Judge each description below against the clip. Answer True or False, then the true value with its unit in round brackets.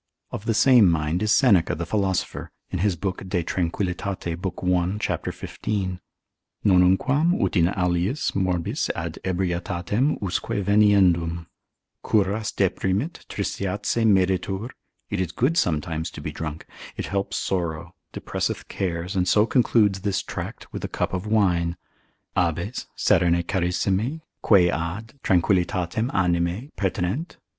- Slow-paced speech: True (130 wpm)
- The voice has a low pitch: True (95 Hz)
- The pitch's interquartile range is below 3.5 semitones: True (3.0 semitones)